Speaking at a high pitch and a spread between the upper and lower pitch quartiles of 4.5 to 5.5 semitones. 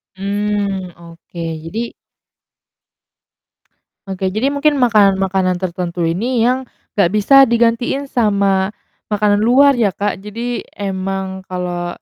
No: high, 200 Hz; average, 3.7 semitones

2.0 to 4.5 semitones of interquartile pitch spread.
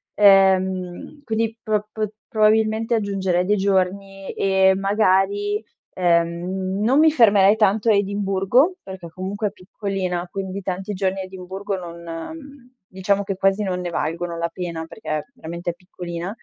Yes: narrow, 2.3 semitones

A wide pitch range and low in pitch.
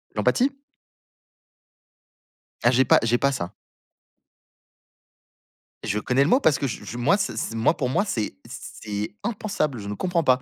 Yes: wide, 6.8 semitones; low, 130 Hz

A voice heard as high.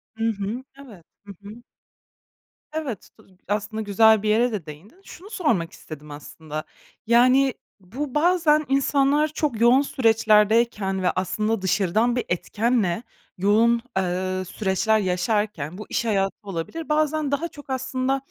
Yes: high, 220 Hz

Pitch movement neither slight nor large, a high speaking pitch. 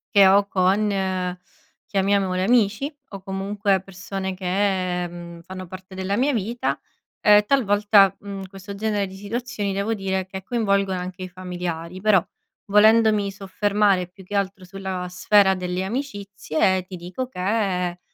No: narrow, 1.8 semitones; high, 195 Hz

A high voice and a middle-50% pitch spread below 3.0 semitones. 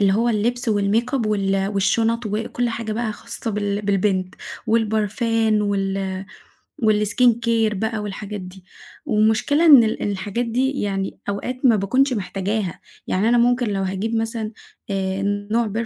Yes: high, 215 Hz; narrow, 2.6 semitones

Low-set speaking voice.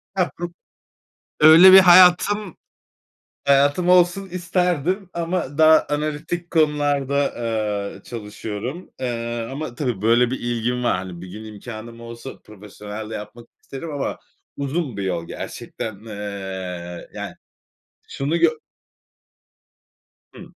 Yes: low, 130 Hz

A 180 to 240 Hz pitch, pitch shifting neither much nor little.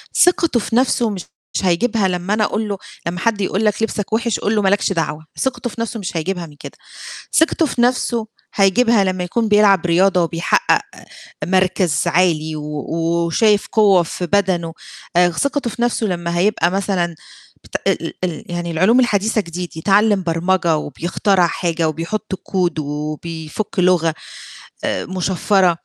Yes: medium, 185 Hz; average, 3.9 semitones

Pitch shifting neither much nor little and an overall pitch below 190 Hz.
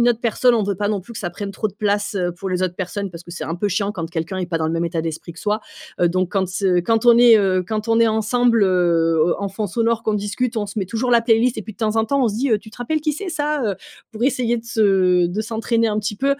No: average, 3.9 semitones; high, 210 Hz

